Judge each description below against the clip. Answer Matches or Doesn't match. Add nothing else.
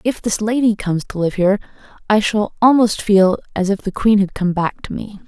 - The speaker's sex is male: Doesn't match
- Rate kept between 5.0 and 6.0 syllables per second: Matches